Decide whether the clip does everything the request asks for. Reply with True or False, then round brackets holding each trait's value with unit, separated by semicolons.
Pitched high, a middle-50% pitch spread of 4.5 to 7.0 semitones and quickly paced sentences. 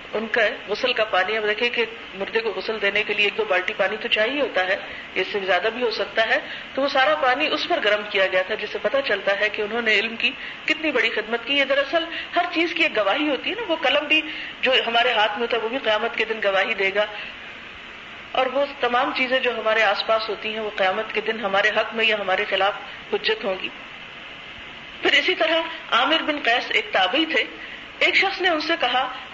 True (225 Hz; 5.0 semitones; 240 wpm)